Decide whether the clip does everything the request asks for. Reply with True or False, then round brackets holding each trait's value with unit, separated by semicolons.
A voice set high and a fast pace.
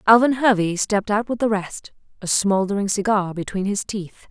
False (205 Hz; 180 wpm)